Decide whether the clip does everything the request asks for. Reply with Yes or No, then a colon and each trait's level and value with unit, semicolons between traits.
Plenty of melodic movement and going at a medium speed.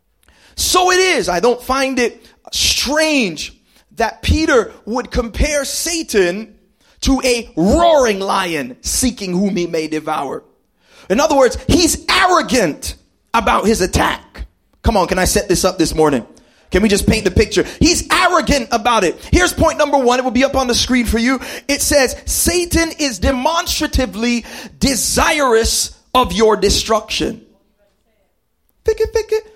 Yes: wide, 6.4 semitones; average, 150 wpm